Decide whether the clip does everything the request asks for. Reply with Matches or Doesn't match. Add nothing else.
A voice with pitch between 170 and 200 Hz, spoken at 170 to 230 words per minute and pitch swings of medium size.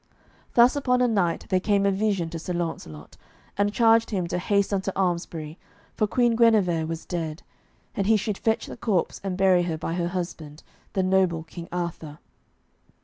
Matches